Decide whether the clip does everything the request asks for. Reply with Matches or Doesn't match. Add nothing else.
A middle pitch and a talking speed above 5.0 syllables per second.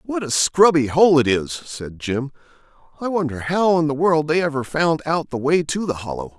Doesn't match